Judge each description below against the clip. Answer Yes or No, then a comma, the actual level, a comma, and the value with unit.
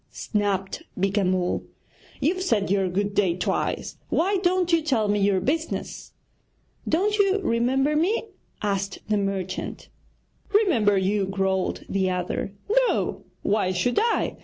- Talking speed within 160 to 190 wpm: No, slow, 135 wpm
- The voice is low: No, high, 205 Hz